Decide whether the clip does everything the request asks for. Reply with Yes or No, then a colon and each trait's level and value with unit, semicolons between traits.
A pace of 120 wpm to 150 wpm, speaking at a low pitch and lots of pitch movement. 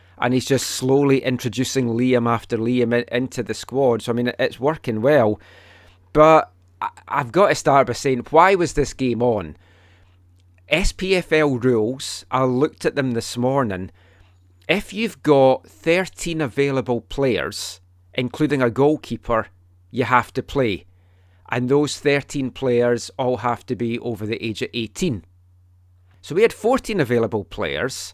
Yes: average, 145 wpm; low, 120 Hz; wide, 6.0 semitones